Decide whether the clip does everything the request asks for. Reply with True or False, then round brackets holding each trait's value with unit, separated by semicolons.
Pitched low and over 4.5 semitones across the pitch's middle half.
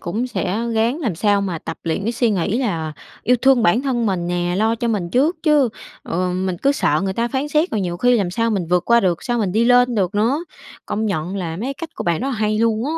False (220 Hz; 5.4 semitones)